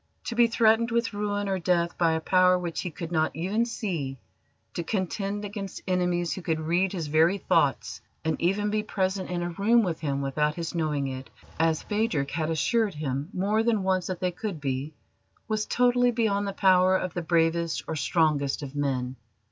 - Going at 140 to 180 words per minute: No, average, 195 wpm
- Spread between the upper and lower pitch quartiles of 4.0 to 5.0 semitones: Yes, average, 4.4 semitones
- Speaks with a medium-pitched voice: Yes, medium, 180 Hz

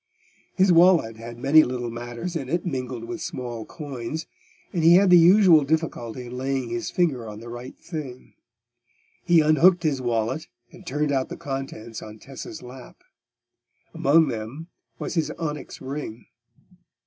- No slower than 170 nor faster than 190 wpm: No, average, 155 wpm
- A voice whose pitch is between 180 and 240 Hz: No, low, 135 Hz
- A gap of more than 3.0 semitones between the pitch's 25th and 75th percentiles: Yes, average, 5.1 semitones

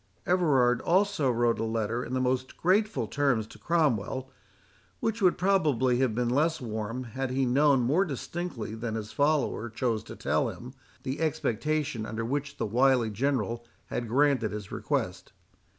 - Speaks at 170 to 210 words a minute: No, average, 160 wpm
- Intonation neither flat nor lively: Yes, average, 4.2 semitones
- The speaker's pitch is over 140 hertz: No, low, 130 Hz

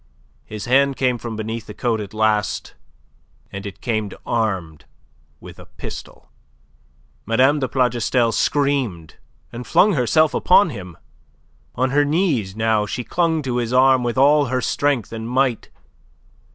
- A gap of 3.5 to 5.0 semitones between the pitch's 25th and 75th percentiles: Yes, average, 3.9 semitones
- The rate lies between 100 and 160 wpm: Yes, average, 145 wpm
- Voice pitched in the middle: No, low, 120 Hz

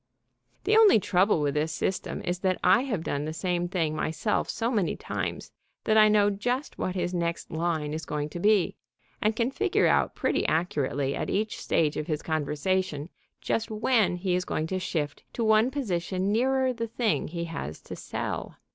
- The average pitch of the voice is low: No, medium, 185 Hz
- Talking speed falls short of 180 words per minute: No, average, 190 wpm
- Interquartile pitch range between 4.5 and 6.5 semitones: Yes, wide, 5.4 semitones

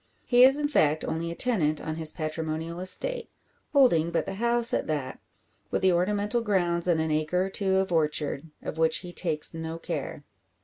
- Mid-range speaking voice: Yes, medium, 170 Hz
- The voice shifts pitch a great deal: No, average, 4.3 semitones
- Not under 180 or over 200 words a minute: Yes, average, 190 wpm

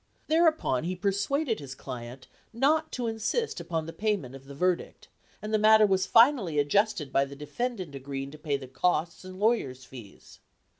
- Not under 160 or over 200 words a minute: Yes, average, 170 wpm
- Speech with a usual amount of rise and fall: No, wide, 8.1 semitones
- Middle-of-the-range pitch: Yes, medium, 180 Hz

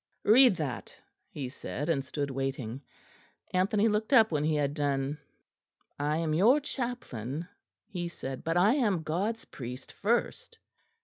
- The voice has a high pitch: No, medium, 160 Hz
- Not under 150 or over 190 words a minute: No, average, 140 wpm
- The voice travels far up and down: Yes, wide, 7.3 semitones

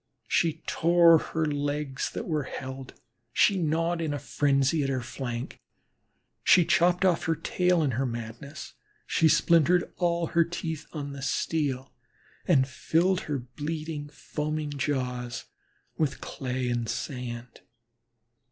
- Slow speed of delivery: Yes, slow, 130 wpm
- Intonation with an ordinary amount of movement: Yes, average, 3.9 semitones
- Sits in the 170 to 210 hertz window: No, medium, 150 Hz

